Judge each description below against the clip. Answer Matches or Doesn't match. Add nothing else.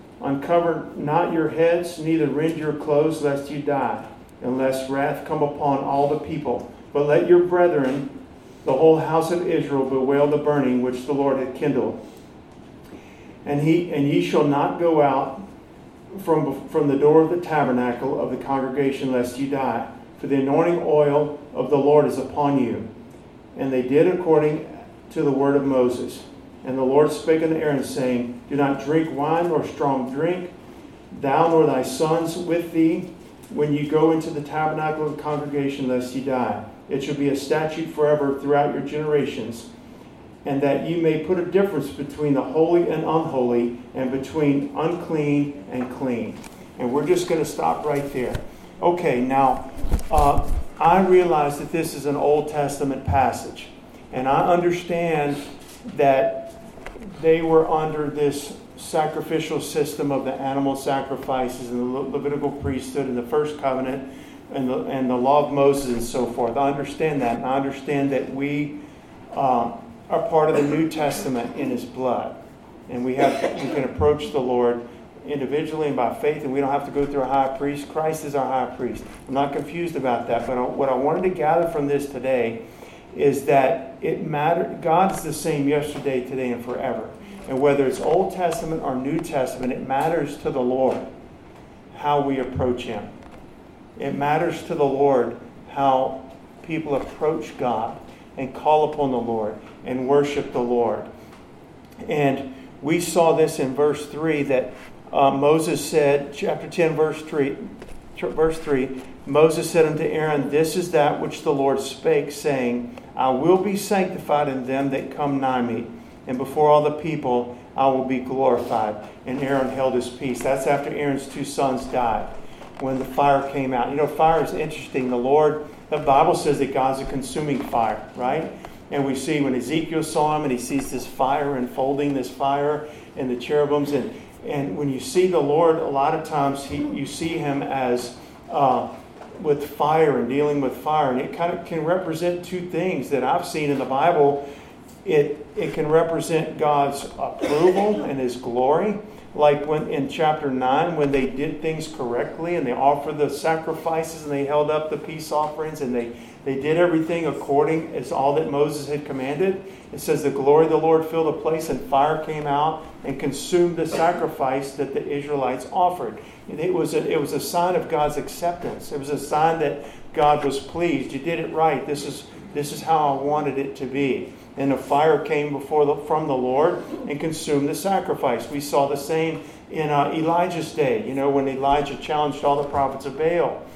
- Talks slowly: Doesn't match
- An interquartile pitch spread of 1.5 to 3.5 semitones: Matches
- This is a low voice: Doesn't match